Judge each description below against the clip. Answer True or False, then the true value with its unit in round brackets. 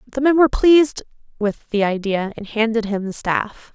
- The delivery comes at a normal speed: True (190 wpm)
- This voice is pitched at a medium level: False (230 Hz)